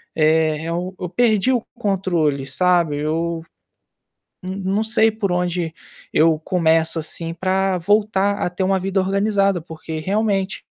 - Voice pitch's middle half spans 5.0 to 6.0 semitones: No, average, 3.3 semitones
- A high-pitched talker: No, medium, 180 Hz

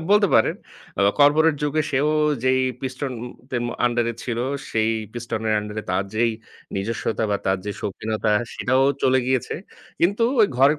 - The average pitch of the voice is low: Yes, low, 125 Hz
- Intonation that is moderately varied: Yes, average, 4.2 semitones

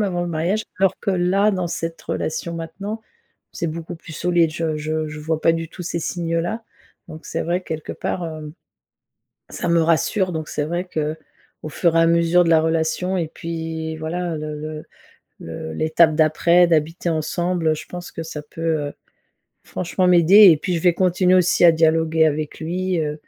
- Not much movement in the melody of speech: Yes, narrow, 2.0 semitones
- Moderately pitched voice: Yes, medium, 165 Hz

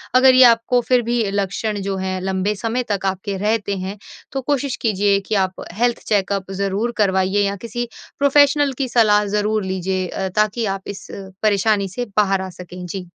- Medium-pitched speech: No, high, 205 Hz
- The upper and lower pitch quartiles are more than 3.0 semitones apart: Yes, average, 3.5 semitones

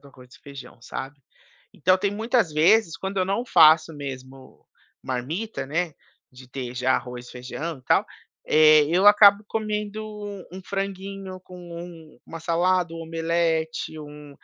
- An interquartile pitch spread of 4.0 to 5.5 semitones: Yes, average, 5.2 semitones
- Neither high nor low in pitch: Yes, medium, 165 Hz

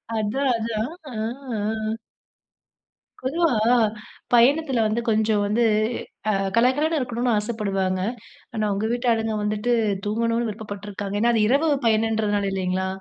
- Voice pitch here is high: Yes, high, 220 Hz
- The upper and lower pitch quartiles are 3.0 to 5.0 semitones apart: No, narrow, 2.6 semitones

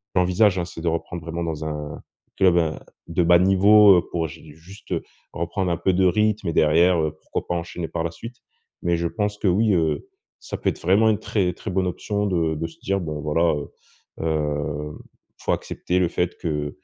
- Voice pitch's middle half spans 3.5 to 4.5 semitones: No, average, 2.8 semitones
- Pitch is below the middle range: Yes, very low, 85 Hz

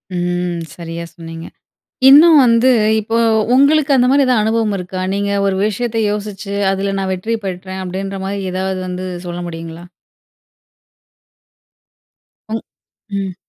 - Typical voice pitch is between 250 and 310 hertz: No, high, 195 Hz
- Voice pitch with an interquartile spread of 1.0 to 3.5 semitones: No, average, 4.0 semitones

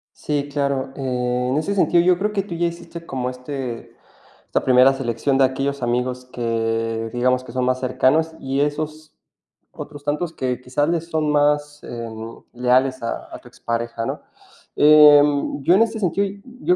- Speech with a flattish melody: No, average, 3.5 semitones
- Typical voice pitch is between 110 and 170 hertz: Yes, low, 135 Hz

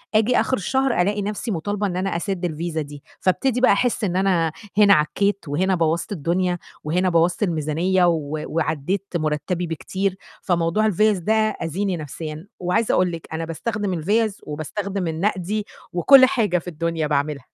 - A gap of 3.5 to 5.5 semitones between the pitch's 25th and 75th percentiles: Yes, average, 3.9 semitones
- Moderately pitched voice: Yes, medium, 180 Hz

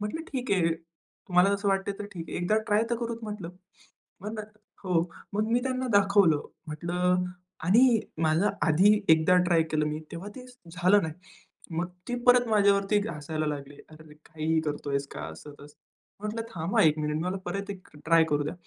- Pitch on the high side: No, medium, 180 Hz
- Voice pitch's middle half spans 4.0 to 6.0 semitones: Yes, average, 4.4 semitones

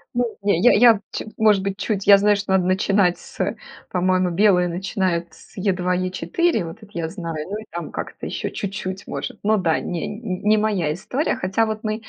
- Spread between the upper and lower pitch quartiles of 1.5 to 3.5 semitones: Yes, average, 2.8 semitones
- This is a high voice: Yes, high, 195 Hz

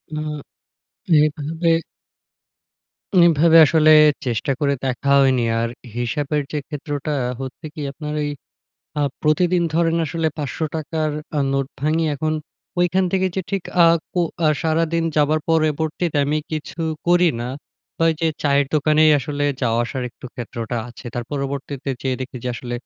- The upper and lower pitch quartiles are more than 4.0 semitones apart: No, average, 3.0 semitones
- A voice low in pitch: No, medium, 150 Hz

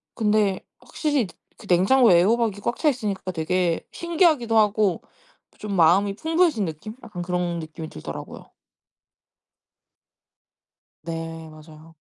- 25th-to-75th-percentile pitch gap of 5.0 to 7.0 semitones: Yes, wide, 5.4 semitones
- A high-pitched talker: Yes, high, 195 Hz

